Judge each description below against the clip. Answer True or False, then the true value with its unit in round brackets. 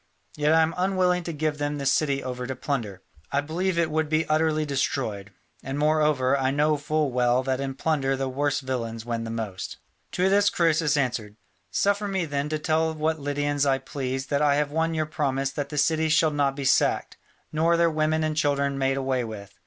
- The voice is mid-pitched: True (145 Hz)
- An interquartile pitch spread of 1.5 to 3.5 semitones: True (2.9 semitones)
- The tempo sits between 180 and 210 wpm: True (205 wpm)